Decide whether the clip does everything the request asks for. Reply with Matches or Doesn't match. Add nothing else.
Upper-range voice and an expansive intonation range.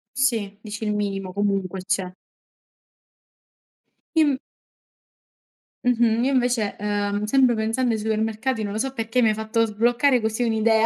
Doesn't match